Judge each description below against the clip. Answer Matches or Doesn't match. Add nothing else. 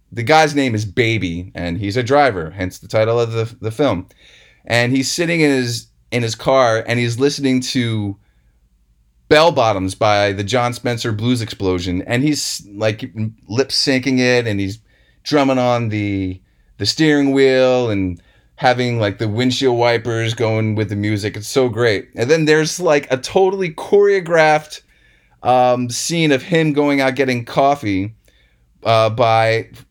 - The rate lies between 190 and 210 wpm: Doesn't match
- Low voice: Matches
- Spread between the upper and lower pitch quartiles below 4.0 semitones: Doesn't match